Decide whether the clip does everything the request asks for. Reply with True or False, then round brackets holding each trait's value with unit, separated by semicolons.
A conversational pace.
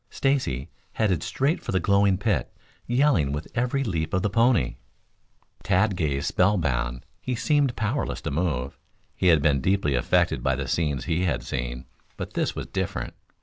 True (165 wpm)